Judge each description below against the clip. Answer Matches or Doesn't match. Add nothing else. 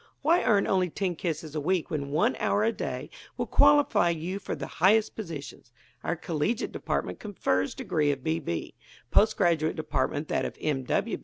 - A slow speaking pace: Doesn't match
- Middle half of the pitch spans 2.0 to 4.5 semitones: Doesn't match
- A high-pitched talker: Doesn't match